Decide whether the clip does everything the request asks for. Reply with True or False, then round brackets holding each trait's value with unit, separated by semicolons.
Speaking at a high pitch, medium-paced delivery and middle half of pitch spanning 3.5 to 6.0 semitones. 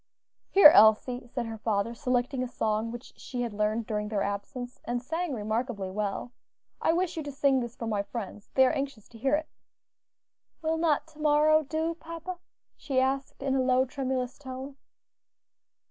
True (255 Hz; 175 wpm; 4.5 semitones)